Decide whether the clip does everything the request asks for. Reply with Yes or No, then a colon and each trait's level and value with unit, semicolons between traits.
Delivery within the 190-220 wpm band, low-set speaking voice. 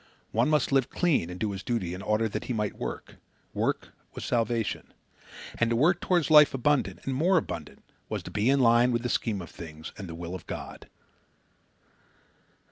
Yes: average, 195 wpm; low, 115 Hz